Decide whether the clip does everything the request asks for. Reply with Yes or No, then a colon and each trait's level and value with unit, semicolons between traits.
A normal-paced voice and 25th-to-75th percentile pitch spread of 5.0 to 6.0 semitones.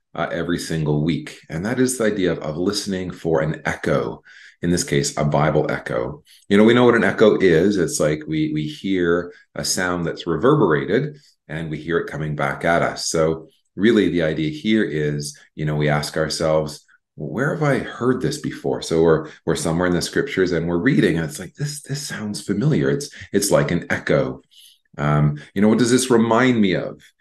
No: fast, 210 wpm; wide, 5.5 semitones